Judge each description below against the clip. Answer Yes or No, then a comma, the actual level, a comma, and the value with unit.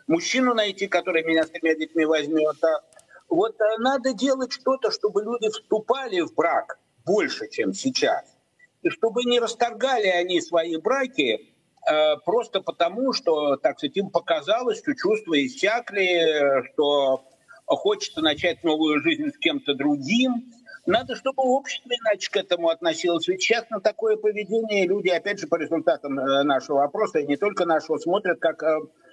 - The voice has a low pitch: No, high, 205 Hz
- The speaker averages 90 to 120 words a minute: No, average, 145 wpm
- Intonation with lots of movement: Yes, wide, 8.0 semitones